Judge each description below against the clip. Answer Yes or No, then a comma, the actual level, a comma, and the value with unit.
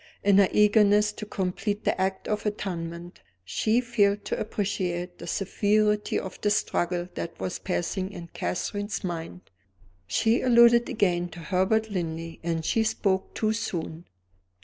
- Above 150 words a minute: No, average, 145 wpm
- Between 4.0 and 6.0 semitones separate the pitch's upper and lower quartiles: No, average, 3.1 semitones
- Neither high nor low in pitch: No, high, 195 Hz